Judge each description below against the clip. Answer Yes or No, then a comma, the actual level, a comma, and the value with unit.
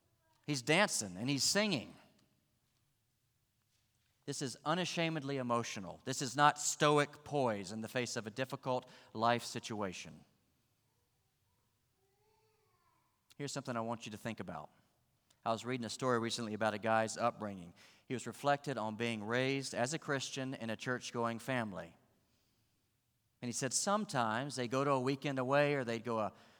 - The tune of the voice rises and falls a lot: No, average, 3.5 semitones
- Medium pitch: No, low, 120 Hz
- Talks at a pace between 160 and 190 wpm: No, average, 150 wpm